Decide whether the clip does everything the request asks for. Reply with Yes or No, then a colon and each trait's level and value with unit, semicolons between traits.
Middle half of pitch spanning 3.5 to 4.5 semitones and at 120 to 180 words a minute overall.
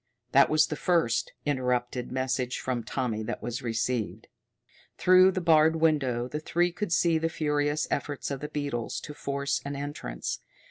Yes: average, 3.9 semitones; average, 165 wpm